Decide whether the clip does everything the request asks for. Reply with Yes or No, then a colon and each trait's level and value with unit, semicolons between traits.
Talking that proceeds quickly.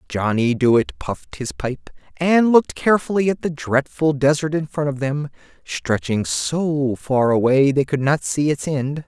No: average, 165 wpm